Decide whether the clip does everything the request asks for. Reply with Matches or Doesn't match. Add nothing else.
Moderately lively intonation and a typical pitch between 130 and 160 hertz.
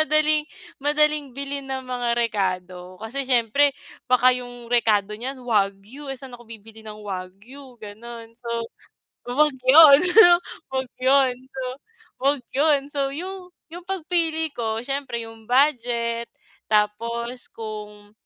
Doesn't match